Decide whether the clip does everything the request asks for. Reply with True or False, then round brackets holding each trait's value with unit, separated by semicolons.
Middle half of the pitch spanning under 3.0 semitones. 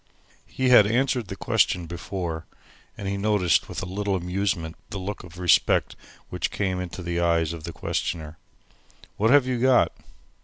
False (3.5 semitones)